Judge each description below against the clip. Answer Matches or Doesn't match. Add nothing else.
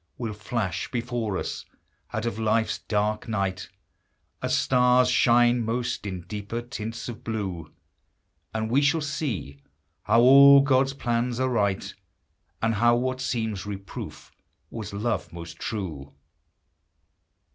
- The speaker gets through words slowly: Matches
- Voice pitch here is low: Matches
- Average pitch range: Matches